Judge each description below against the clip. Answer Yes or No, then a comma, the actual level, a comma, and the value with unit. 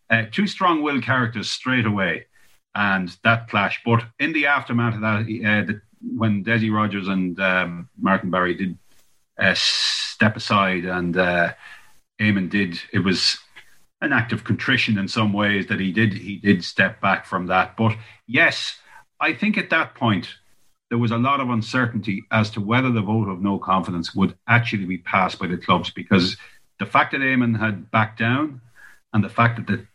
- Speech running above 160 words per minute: Yes, average, 185 wpm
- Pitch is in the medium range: No, low, 110 Hz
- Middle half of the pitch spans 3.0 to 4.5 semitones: Yes, average, 3.5 semitones